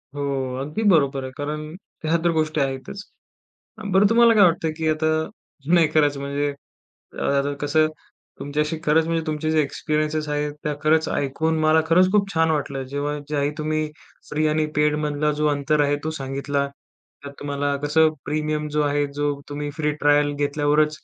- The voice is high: No, medium, 150 Hz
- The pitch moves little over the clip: Yes, narrow, 1.5 semitones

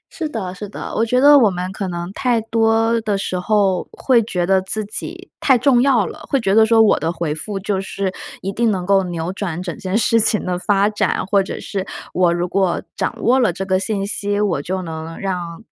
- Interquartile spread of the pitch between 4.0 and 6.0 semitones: No, average, 3.5 semitones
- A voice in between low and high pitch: No, high, 195 Hz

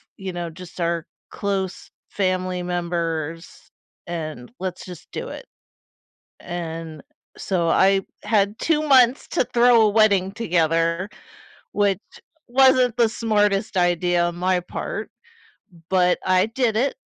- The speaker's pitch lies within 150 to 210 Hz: Yes, medium, 185 Hz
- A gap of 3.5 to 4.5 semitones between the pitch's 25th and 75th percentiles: Yes, average, 3.8 semitones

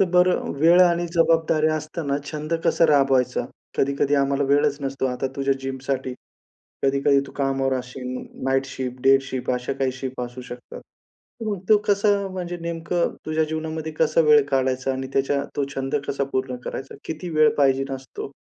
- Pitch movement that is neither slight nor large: Yes, average, 3.0 semitones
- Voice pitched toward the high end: No, medium, 140 Hz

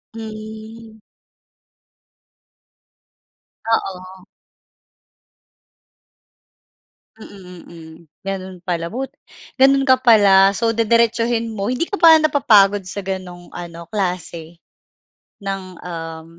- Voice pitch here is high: Yes, high, 200 Hz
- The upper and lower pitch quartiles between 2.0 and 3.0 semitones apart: No, average, 3.9 semitones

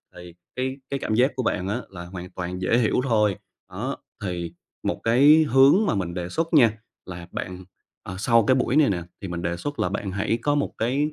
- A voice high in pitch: No, low, 105 Hz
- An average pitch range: No, wide, 6.6 semitones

